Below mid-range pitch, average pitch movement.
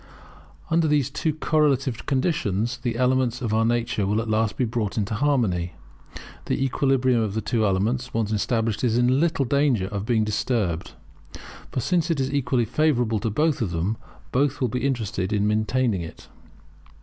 Yes: low, 120 Hz; average, 3.9 semitones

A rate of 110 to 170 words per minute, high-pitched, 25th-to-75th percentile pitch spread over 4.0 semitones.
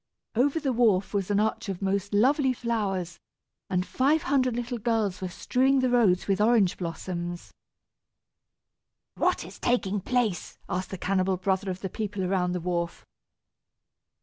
Yes: average, 150 wpm; high, 200 Hz; average, 4.7 semitones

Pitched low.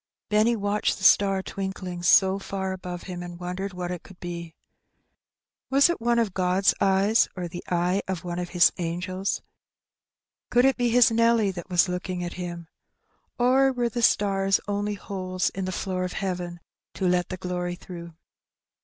No: medium, 185 Hz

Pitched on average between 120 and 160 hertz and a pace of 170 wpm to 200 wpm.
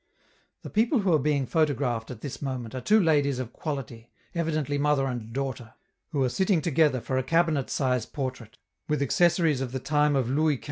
Yes: medium, 140 Hz; average, 195 wpm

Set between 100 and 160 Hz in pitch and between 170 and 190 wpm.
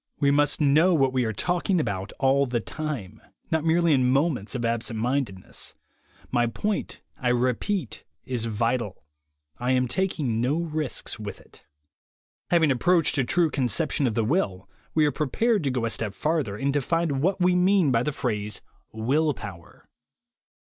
Yes: low, 135 Hz; average, 175 wpm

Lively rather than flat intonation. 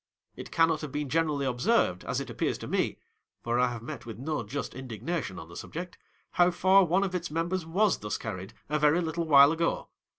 Yes: wide, 5.7 semitones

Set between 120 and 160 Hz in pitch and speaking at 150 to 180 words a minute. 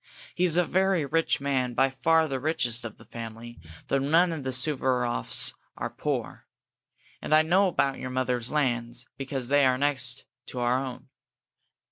Yes: low, 135 Hz; average, 170 wpm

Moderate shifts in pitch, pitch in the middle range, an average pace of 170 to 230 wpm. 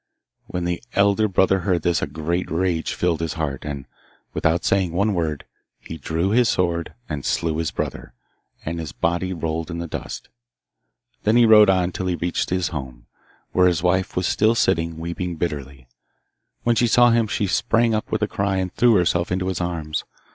No: average, 3.0 semitones; very low, 90 Hz; average, 190 wpm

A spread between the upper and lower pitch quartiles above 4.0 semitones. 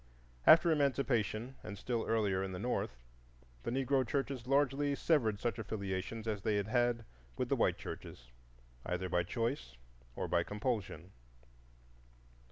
Yes: average, 5.1 semitones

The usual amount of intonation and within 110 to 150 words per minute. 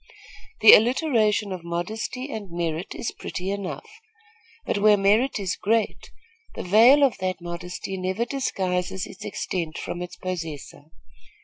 Yes: average, 3.7 semitones; slow, 135 wpm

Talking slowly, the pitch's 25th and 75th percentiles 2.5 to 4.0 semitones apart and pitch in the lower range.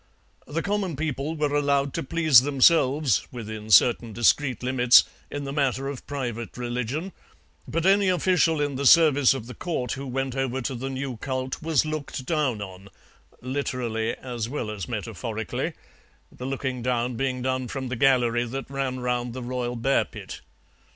No: average, 165 wpm; average, 2.8 semitones; low, 130 Hz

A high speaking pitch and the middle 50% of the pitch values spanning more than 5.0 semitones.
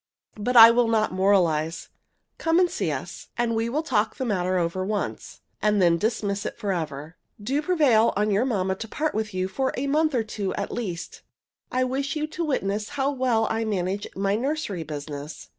Yes: high, 215 Hz; wide, 5.5 semitones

